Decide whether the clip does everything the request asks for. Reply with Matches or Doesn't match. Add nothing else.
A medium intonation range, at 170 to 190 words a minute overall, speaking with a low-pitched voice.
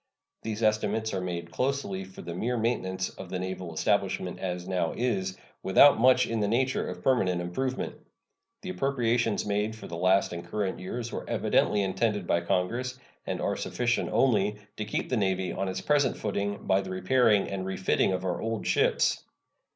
Matches